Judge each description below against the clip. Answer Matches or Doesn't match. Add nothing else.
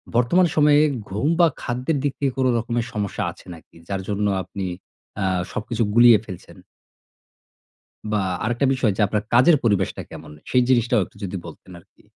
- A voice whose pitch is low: Matches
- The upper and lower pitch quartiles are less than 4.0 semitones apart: Doesn't match